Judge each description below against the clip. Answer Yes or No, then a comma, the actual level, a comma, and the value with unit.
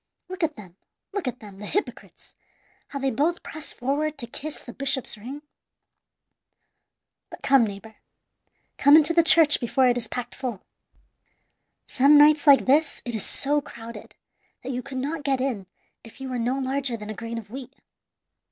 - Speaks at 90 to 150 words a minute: No, average, 175 wpm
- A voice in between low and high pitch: No, very high, 265 Hz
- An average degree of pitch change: Yes, average, 3.8 semitones